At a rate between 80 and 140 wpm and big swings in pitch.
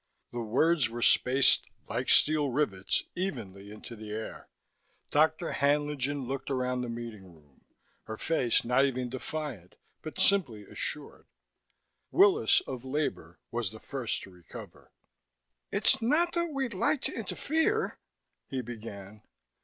Yes: slow, 135 wpm; wide, 6.1 semitones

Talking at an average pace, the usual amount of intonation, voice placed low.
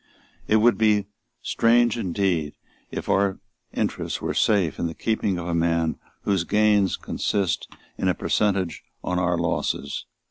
Yes: average, 145 wpm; average, 3.9 semitones; very low, 95 Hz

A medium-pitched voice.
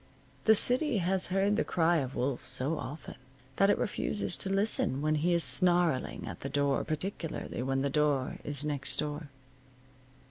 Yes: medium, 155 Hz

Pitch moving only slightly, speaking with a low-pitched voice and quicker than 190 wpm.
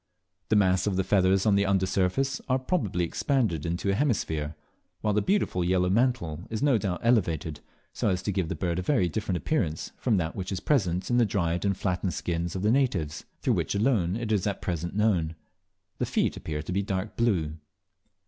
No: average, 4.1 semitones; very low, 95 Hz; fast, 205 wpm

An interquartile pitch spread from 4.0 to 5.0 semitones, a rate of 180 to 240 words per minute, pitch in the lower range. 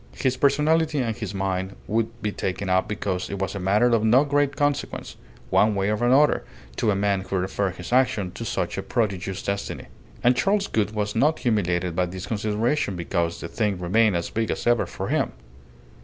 Yes: average, 4.3 semitones; average, 200 wpm; low, 105 Hz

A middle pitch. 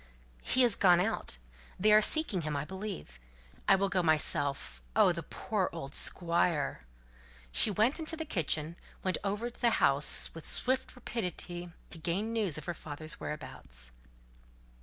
Yes: medium, 180 Hz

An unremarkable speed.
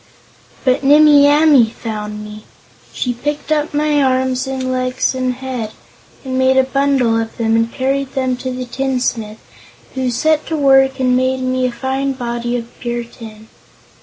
Yes: average, 165 wpm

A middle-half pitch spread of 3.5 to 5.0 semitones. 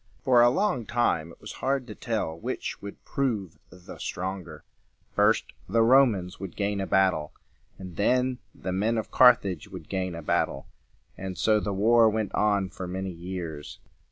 Yes: average, 4.0 semitones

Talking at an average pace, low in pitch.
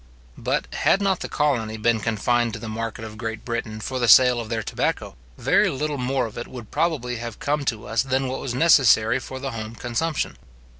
No: fast, 210 wpm; low, 120 Hz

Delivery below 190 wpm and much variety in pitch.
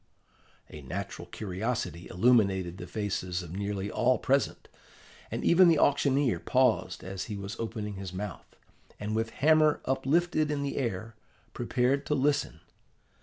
Yes: average, 140 wpm; wide, 6.1 semitones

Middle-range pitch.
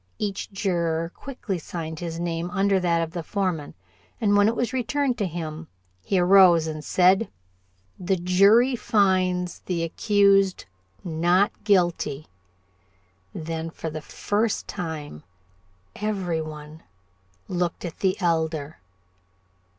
Yes: medium, 180 Hz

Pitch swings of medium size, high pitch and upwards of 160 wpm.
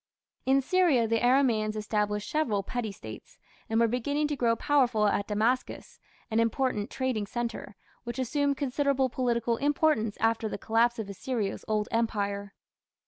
No: average, 3.6 semitones; high, 230 Hz; average, 145 wpm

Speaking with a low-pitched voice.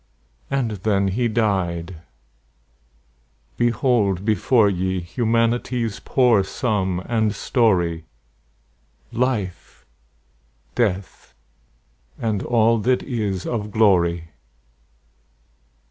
Yes: low, 105 Hz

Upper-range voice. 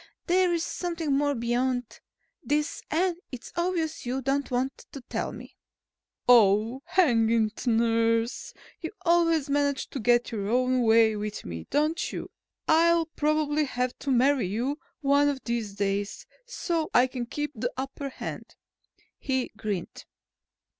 Yes: very high, 260 Hz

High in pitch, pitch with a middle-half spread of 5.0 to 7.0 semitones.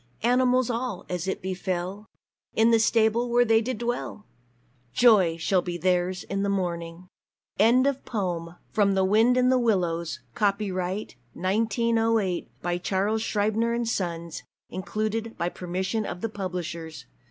No: high, 200 Hz; average, 4.2 semitones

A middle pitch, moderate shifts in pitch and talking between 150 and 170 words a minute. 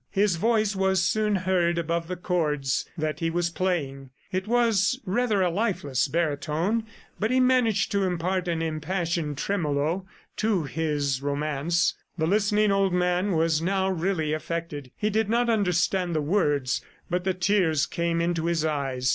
Yes: medium, 175 Hz; average, 4.1 semitones; average, 155 wpm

